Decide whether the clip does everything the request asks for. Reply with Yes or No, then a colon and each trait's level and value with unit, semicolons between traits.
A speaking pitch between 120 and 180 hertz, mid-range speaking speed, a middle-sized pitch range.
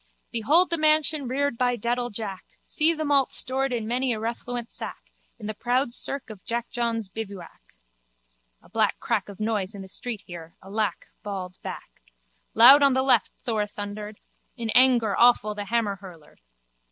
No: high, 230 Hz; average, 160 wpm; average, 3.6 semitones